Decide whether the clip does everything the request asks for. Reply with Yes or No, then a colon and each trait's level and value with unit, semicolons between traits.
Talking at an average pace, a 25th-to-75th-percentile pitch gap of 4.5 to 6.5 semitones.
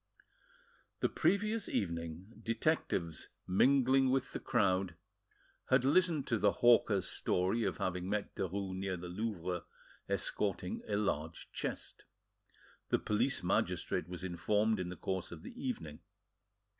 No: slow, 130 wpm; average, 5.2 semitones